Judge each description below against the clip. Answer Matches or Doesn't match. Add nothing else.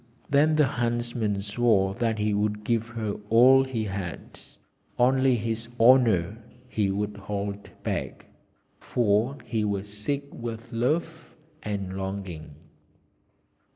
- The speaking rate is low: Matches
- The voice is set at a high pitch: Doesn't match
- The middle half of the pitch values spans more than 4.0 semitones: Doesn't match